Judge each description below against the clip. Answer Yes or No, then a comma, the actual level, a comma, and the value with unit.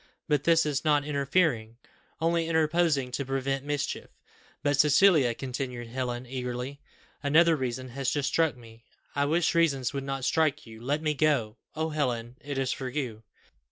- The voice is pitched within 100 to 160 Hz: Yes, medium, 140 Hz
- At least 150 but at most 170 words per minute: Yes, average, 160 wpm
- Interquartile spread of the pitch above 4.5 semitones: No, average, 3.4 semitones